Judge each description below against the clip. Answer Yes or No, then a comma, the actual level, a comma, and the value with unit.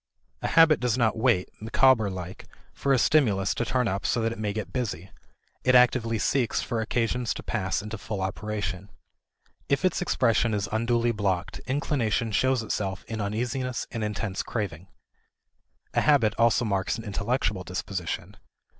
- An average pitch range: Yes, average, 3.6 semitones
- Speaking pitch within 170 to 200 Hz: No, low, 110 Hz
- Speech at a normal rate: Yes, average, 160 wpm